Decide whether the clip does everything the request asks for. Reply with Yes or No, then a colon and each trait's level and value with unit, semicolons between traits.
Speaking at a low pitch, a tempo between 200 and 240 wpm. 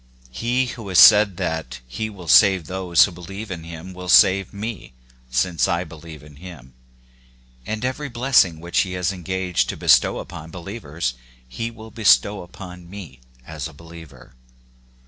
No: very low, 90 Hz; average, 165 wpm